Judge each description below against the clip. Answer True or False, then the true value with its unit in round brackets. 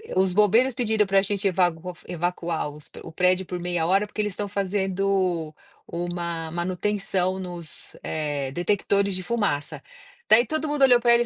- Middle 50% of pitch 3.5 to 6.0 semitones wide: False (3.0 semitones)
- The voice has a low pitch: False (185 Hz)